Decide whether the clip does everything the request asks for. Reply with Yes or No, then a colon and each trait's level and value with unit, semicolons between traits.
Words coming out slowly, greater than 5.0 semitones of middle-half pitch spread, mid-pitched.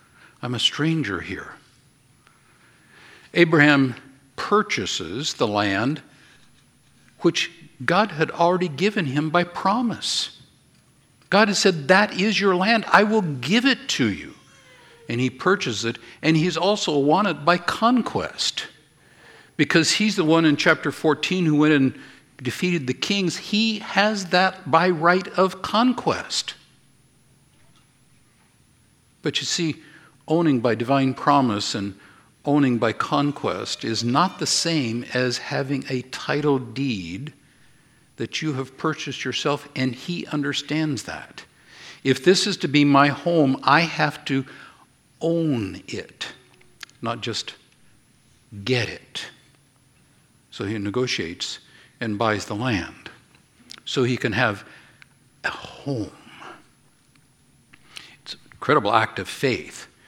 Yes: slow, 125 wpm; wide, 5.6 semitones; medium, 150 Hz